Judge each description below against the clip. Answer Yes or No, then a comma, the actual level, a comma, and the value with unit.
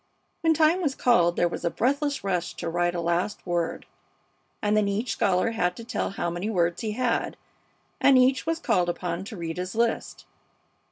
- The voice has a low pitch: No, high, 200 Hz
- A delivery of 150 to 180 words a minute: No, average, 190 wpm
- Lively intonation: Yes, wide, 6.2 semitones